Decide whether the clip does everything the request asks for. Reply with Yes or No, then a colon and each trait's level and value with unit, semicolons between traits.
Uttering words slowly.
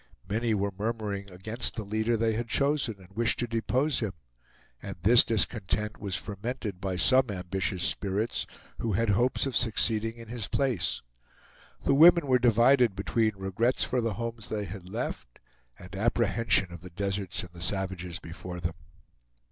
No: average, 165 wpm